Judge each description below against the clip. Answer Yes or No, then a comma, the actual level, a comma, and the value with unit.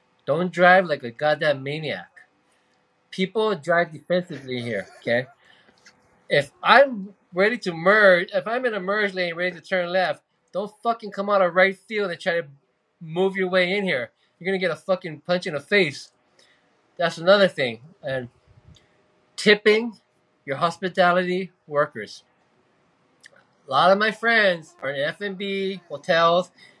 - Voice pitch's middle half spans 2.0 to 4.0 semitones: Yes, average, 3.4 semitones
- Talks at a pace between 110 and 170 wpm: Yes, average, 150 wpm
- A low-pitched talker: No, medium, 185 Hz